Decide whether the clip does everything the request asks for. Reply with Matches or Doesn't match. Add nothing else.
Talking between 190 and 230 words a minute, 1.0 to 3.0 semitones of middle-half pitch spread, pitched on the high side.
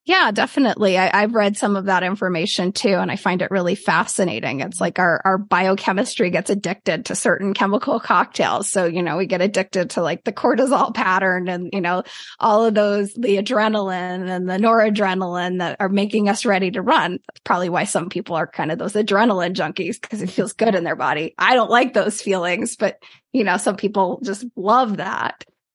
Matches